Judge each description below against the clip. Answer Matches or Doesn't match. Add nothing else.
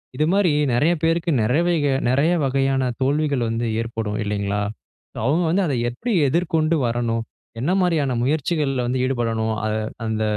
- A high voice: Doesn't match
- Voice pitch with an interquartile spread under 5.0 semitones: Doesn't match